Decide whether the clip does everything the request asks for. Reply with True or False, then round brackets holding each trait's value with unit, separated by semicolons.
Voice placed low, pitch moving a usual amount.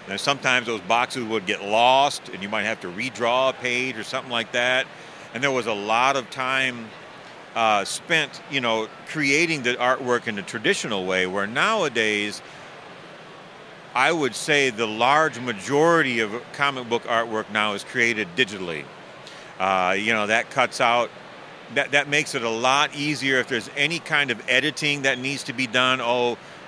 True (125 Hz; 3.6 semitones)